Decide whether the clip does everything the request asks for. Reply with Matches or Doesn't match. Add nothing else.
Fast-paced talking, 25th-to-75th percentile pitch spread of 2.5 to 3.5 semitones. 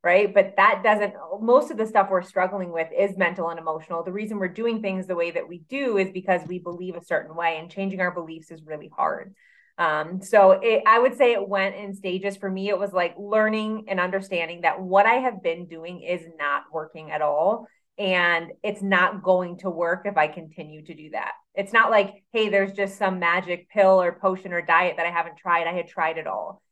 Matches